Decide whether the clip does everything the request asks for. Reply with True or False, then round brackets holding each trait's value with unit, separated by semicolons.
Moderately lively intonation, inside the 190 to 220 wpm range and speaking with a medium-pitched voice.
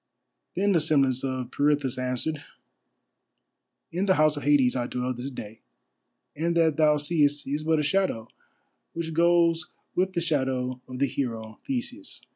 False (4.6 semitones; 155 wpm; 145 Hz)